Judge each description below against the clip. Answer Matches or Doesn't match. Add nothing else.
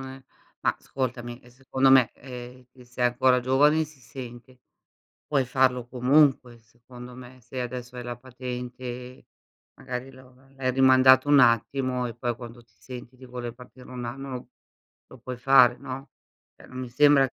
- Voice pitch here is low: Matches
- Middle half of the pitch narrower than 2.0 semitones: Matches